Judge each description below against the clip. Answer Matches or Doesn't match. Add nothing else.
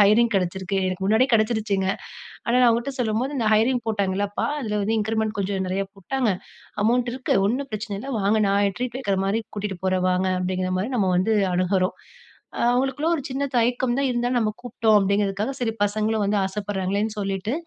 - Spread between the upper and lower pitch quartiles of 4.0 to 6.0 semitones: Doesn't match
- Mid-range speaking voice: Doesn't match